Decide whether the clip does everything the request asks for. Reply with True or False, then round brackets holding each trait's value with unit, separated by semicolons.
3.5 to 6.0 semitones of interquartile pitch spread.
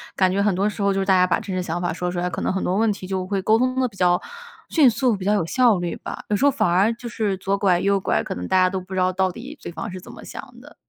False (2.6 semitones)